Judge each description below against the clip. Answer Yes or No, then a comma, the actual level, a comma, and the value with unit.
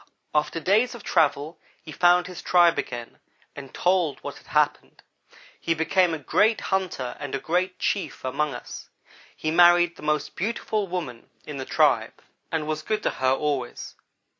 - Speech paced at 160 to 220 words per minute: Yes, average, 165 wpm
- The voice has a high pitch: No, medium, 165 Hz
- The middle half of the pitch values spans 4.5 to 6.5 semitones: No, average, 4.1 semitones